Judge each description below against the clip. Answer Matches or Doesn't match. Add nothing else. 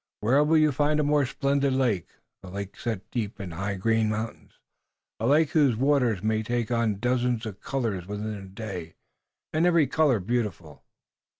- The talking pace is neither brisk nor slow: Matches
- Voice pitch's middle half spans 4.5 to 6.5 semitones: Matches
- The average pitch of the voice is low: Matches